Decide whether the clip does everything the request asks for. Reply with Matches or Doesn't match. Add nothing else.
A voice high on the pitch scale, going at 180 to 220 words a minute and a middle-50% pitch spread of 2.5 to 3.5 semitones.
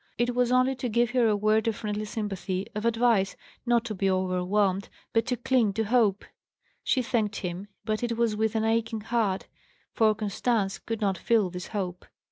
Matches